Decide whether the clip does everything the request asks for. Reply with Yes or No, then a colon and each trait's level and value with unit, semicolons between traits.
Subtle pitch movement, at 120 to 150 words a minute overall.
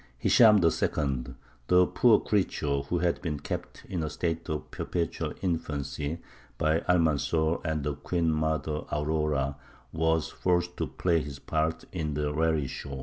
Yes: narrow, 2.2 semitones; average, 145 wpm